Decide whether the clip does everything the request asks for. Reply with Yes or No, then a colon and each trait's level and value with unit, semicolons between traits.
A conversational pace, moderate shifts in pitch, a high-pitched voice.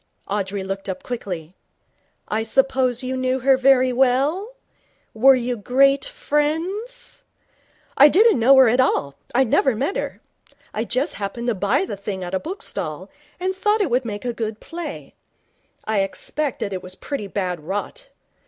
No: average, 160 wpm; wide, 6.1 semitones; very high, 255 Hz